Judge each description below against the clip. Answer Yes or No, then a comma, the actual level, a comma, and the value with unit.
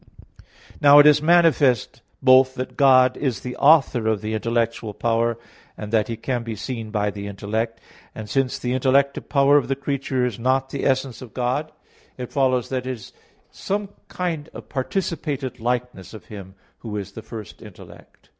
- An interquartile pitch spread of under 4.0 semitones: Yes, average, 3.4 semitones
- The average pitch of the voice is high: No, low, 125 Hz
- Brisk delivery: No, average, 175 wpm